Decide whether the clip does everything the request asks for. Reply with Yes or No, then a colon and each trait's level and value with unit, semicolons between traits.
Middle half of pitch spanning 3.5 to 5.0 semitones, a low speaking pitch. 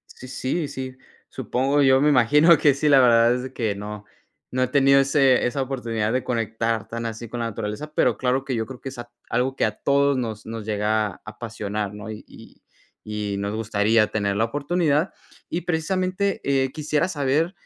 Yes: average, 4.2 semitones; low, 125 Hz